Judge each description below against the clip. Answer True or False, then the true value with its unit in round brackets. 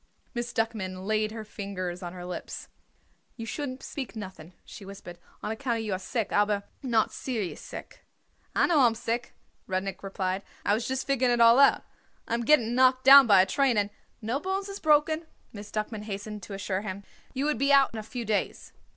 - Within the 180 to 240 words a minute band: True (205 wpm)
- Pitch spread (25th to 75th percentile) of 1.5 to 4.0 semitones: False (4.5 semitones)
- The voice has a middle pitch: False (220 Hz)